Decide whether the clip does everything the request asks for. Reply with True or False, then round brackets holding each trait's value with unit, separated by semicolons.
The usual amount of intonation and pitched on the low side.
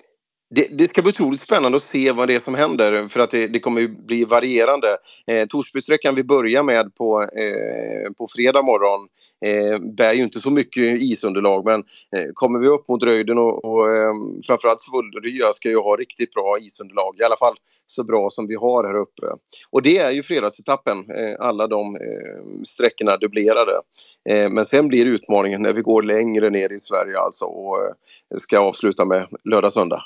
True (4.1 semitones; 115 Hz)